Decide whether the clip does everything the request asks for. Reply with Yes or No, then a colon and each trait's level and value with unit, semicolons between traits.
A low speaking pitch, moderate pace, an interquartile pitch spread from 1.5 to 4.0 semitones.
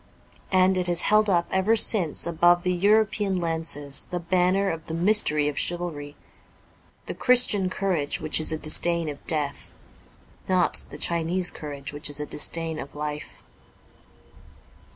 No: medium, 170 Hz; average, 150 wpm; average, 3.6 semitones